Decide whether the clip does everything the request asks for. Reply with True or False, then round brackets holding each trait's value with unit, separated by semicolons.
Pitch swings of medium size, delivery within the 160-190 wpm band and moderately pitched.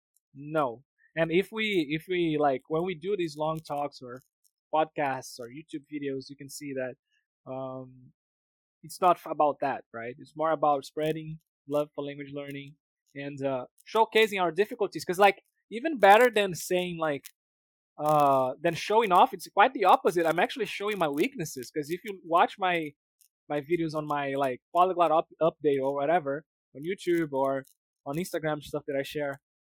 True (4.2 semitones; 170 wpm; 155 Hz)